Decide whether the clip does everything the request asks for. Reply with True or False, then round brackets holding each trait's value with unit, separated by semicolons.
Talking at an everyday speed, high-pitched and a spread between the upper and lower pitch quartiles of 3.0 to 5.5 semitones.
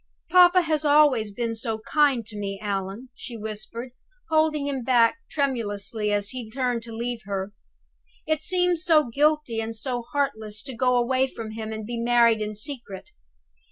True (165 wpm; 235 Hz; 4.5 semitones)